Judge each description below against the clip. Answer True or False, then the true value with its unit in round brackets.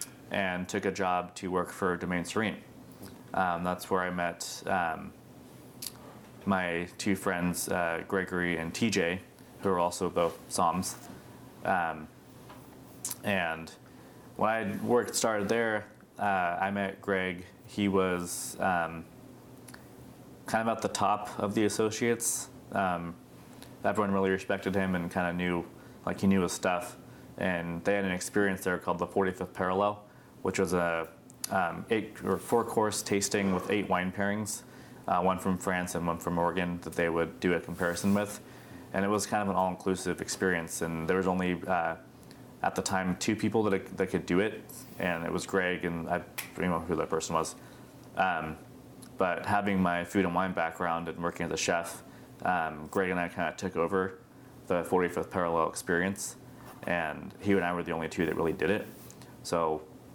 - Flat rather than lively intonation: True (2.3 semitones)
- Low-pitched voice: True (95 Hz)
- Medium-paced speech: True (175 wpm)